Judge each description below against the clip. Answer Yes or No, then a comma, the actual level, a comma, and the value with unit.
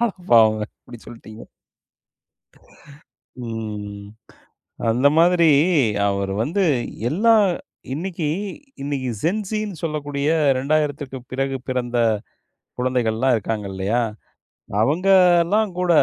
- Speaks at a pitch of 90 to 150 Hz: Yes, medium, 140 Hz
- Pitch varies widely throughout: Yes, wide, 7.4 semitones